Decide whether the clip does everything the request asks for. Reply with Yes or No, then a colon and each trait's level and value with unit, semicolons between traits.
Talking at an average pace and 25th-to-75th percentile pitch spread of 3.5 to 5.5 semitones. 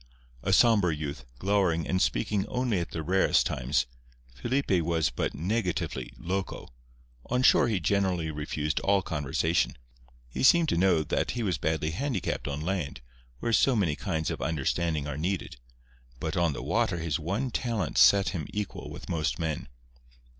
Yes: average, 160 wpm; average, 4.4 semitones